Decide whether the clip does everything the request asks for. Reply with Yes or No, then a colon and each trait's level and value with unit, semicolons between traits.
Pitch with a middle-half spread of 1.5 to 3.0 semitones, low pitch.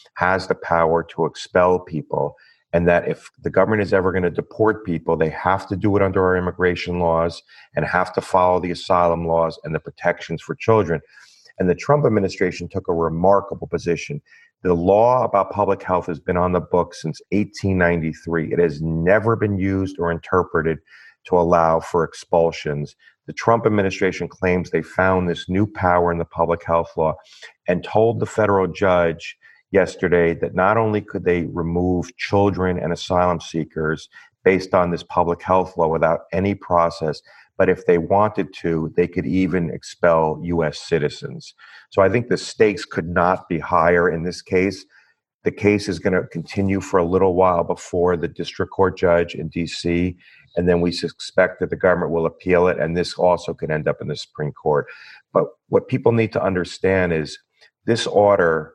Yes: narrow, 2.4 semitones; very low, 90 Hz